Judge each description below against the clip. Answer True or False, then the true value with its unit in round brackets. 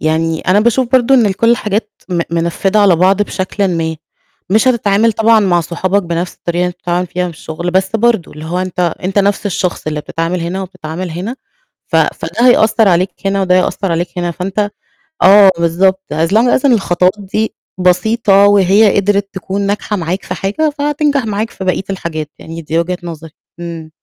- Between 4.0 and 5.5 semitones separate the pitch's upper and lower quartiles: False (3.3 semitones)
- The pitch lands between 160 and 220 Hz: True (190 Hz)